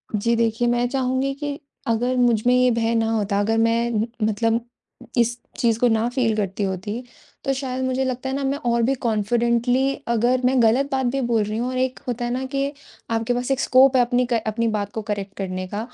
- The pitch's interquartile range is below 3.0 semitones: Yes, narrow, 2.4 semitones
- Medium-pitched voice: No, high, 235 Hz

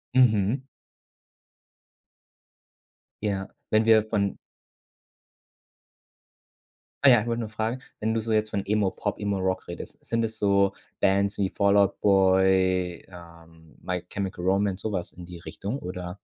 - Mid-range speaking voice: No, low, 100 Hz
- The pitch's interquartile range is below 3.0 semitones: Yes, narrow, 2.5 semitones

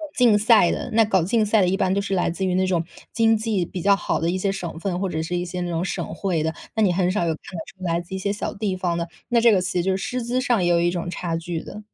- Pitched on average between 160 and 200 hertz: Yes, medium, 185 Hz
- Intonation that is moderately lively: Yes, average, 3.1 semitones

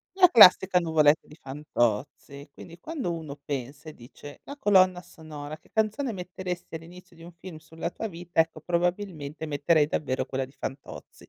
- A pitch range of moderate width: Yes, average, 3.7 semitones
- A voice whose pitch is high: No, medium, 165 Hz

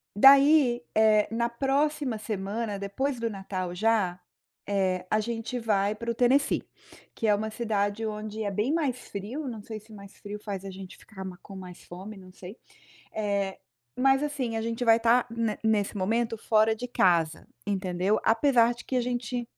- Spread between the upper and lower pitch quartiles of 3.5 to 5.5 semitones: No, average, 3.1 semitones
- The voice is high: Yes, high, 220 Hz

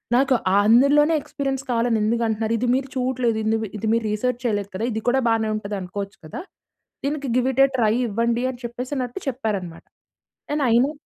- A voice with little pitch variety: No, average, 3.1 semitones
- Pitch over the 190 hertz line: Yes, high, 235 Hz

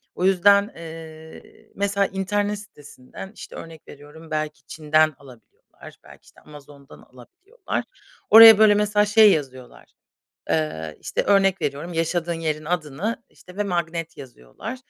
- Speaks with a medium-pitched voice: Yes, medium, 165 Hz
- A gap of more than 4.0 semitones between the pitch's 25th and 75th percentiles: Yes, average, 5.2 semitones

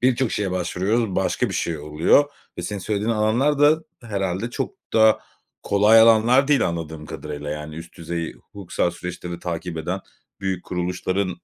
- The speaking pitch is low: Yes, very low, 95 Hz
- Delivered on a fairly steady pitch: No, average, 4.8 semitones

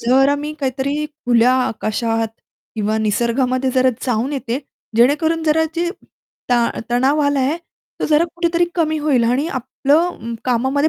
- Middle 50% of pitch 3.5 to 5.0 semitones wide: Yes, average, 4.0 semitones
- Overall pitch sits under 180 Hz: No, very high, 265 Hz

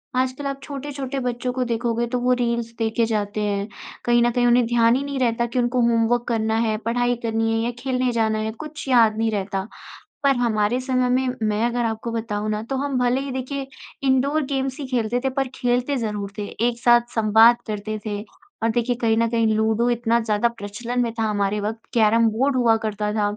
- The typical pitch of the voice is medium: No, high, 235 Hz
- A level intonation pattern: Yes, narrow, 2.3 semitones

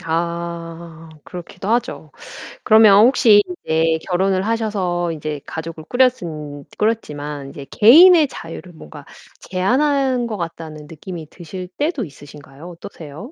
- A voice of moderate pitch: Yes, medium, 175 Hz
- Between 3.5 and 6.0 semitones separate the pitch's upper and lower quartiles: Yes, wide, 5.5 semitones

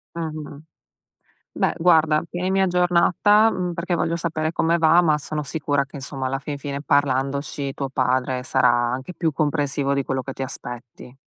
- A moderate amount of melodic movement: Yes, average, 3.8 semitones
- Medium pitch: Yes, medium, 145 Hz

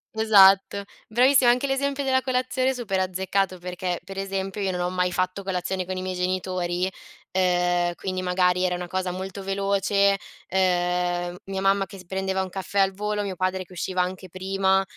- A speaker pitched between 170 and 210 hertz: Yes, high, 190 Hz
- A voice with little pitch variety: Yes, narrow, 1.5 semitones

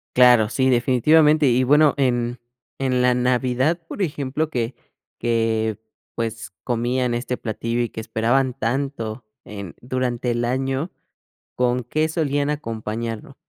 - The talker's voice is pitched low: Yes, low, 125 Hz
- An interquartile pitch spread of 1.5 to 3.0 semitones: Yes, narrow, 2.6 semitones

